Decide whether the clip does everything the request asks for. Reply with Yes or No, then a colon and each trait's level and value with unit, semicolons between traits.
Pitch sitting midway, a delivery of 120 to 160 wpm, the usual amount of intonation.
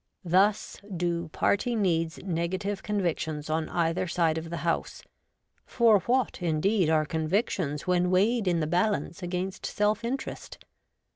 Yes: medium, 180 Hz; average, 140 wpm; average, 3.7 semitones